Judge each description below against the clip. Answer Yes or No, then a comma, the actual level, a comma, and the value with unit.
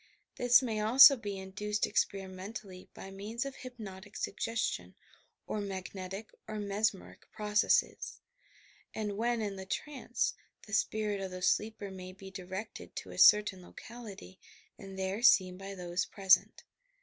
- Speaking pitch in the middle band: No, high, 200 Hz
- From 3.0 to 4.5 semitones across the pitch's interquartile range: No, narrow, 2.4 semitones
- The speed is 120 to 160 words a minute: Yes, average, 150 wpm